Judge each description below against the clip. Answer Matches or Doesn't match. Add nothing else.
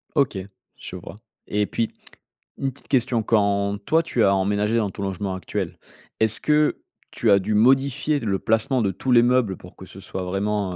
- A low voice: Matches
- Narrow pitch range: Doesn't match